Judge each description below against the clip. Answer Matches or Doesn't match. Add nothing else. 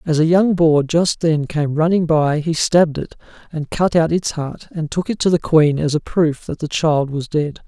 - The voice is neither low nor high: Matches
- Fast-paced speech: Matches